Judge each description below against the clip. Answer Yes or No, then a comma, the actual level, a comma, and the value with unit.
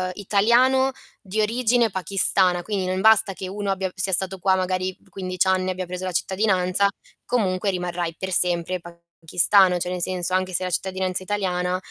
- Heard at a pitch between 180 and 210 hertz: Yes, medium, 185 Hz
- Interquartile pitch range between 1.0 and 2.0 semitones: Yes, narrow, 1.6 semitones